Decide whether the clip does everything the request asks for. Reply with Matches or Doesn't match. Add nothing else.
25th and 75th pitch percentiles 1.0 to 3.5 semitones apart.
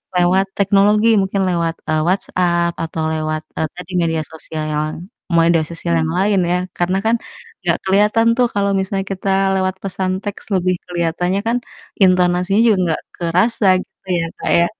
Matches